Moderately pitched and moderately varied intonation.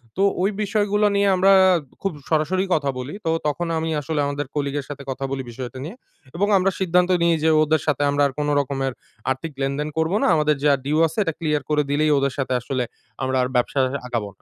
Yes: medium, 150 Hz; average, 3.4 semitones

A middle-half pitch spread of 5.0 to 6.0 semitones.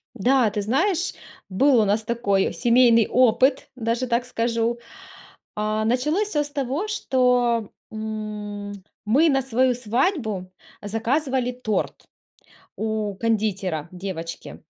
No: average, 3.5 semitones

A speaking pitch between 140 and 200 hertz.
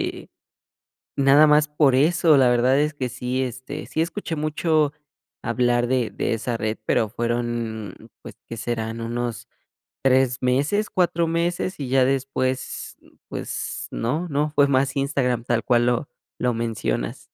No: low, 130 Hz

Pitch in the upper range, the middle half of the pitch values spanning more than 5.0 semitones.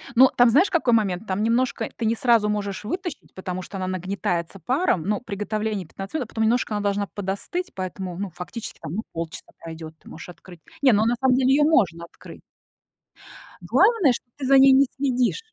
Yes: high, 210 Hz; wide, 5.5 semitones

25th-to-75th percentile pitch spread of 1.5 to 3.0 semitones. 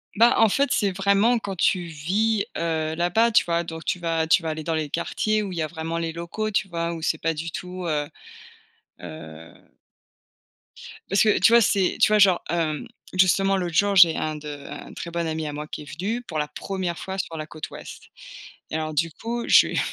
No: average, 3.8 semitones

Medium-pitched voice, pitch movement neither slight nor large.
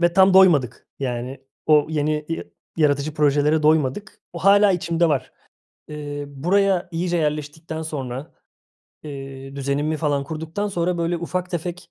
Yes: medium, 155 Hz; average, 3.2 semitones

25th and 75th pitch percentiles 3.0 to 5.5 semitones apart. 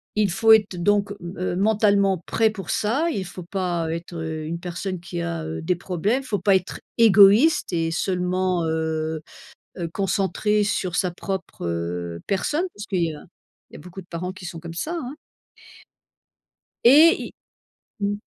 Yes: average, 3.6 semitones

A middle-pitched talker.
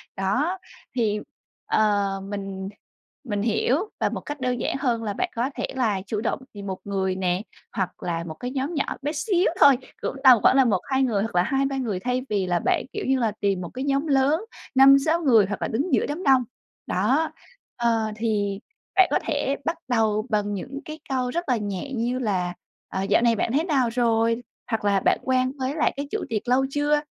No: high, 235 Hz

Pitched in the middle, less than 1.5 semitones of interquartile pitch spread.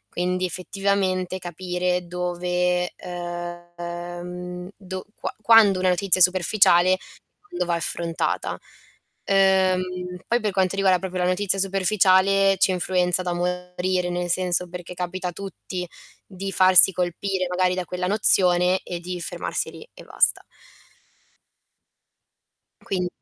Yes: medium, 180 Hz; narrow, 1.0 semitones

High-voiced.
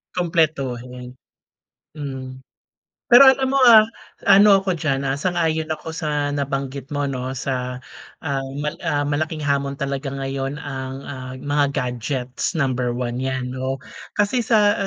No: medium, 140 Hz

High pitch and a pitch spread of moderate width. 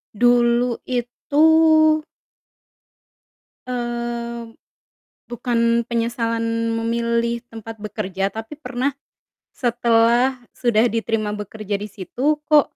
No: high, 235 Hz; narrow, 1.2 semitones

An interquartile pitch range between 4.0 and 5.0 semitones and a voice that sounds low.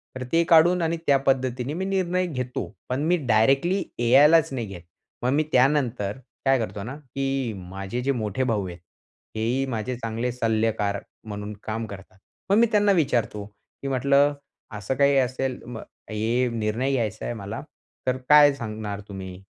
Yes: average, 4.3 semitones; low, 125 Hz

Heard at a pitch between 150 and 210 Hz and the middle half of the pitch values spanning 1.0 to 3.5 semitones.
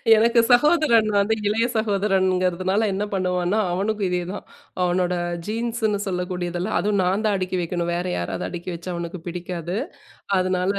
Yes: medium, 185 Hz; average, 2.8 semitones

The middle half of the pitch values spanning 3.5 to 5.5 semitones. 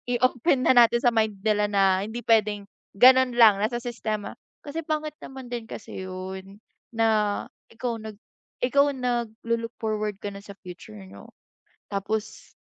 No: average, 3.1 semitones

